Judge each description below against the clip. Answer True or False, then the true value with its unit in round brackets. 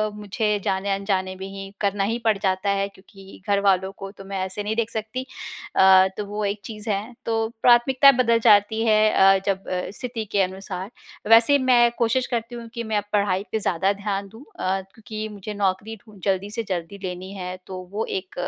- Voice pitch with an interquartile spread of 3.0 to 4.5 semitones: False (2.4 semitones)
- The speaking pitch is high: True (200 Hz)